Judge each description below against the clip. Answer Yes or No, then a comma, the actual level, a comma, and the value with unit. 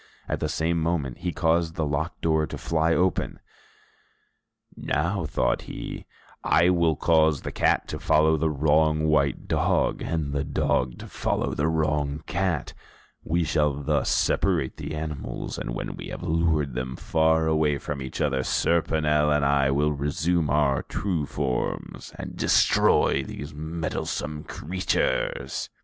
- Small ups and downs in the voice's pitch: Yes, narrow, 2.1 semitones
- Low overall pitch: Yes, very low, 75 Hz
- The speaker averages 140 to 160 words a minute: Yes, average, 150 wpm